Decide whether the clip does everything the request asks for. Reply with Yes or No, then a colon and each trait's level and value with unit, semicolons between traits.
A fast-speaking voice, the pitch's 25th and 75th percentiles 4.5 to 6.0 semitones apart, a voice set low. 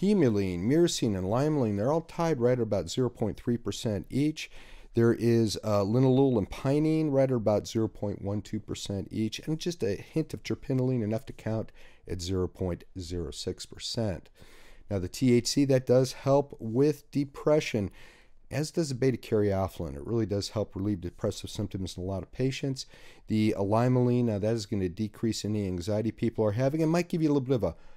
No: average, 175 wpm; average, 5.0 semitones; low, 115 Hz